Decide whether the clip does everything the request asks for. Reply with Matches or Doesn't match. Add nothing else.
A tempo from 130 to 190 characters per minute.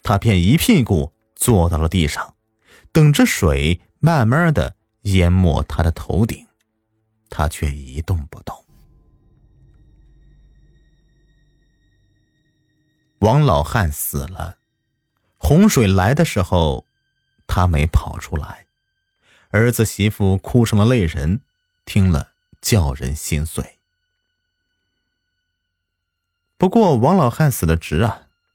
Matches